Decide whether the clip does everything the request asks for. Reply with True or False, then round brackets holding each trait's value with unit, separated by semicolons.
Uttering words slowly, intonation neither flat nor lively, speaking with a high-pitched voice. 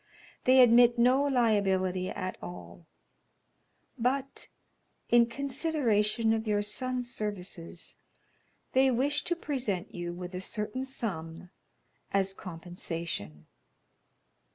False (100 wpm; 5.7 semitones; 215 Hz)